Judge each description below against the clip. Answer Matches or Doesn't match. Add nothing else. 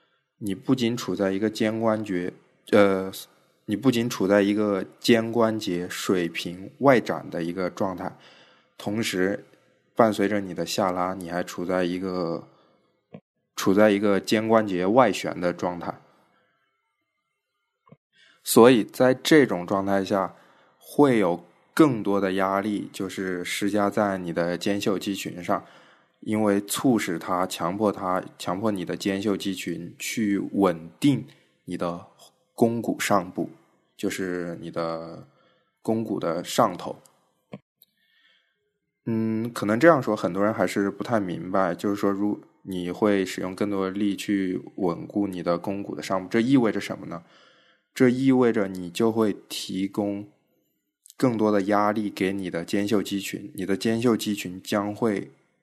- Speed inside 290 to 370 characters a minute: Doesn't match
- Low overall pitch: Matches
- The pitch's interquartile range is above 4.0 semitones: Doesn't match